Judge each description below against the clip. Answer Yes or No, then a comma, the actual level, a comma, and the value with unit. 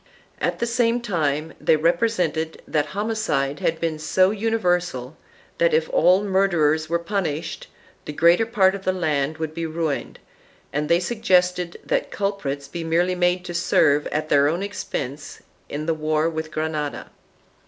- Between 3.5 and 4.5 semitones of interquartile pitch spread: Yes, average, 4.0 semitones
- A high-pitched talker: No, medium, 170 Hz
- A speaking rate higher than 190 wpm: No, average, 160 wpm